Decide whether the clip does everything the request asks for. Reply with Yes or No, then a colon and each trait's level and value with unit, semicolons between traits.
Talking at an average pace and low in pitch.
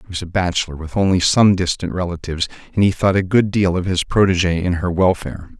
No: fast, 225 wpm; very low, 90 Hz